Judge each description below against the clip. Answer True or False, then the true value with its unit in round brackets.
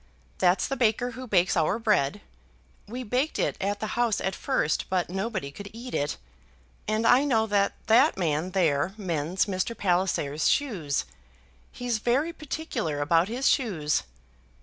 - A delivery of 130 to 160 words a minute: True (150 wpm)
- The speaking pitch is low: False (205 Hz)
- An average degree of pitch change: False (5.7 semitones)